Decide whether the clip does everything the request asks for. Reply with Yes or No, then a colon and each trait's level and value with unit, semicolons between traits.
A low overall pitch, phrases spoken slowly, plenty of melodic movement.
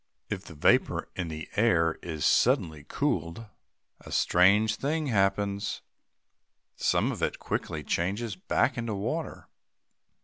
No: low, 100 Hz; slow, 125 wpm; average, 4.7 semitones